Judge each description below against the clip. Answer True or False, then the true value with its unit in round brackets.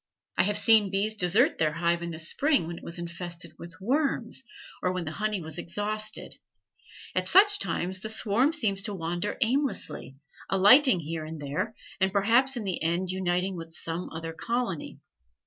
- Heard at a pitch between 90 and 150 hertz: False (190 Hz)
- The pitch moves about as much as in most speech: True (4.6 semitones)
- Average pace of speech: True (175 wpm)